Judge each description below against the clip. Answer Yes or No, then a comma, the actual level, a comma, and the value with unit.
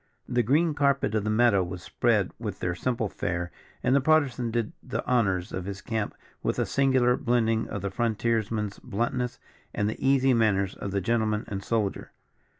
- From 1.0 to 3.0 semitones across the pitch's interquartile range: No, average, 3.8 semitones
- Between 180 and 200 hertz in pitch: No, low, 115 Hz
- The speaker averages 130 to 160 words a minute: No, average, 185 wpm